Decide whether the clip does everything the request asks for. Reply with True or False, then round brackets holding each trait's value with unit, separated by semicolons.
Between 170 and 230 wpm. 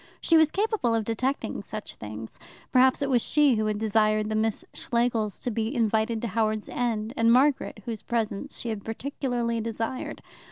True (175 wpm)